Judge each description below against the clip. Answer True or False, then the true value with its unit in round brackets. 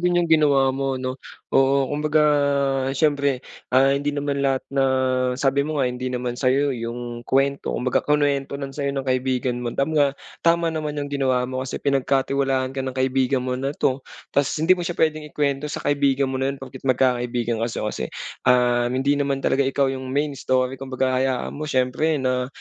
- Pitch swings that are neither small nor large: False (1.8 semitones)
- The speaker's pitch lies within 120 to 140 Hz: True (135 Hz)